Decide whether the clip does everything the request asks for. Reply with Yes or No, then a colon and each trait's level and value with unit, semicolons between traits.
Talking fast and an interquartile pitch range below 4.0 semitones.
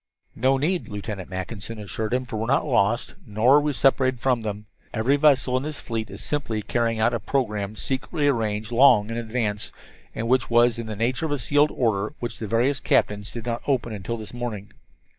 Yes: fast, 210 wpm; average, 3.4 semitones